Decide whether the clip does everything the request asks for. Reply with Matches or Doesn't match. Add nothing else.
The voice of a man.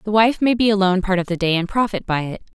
Doesn't match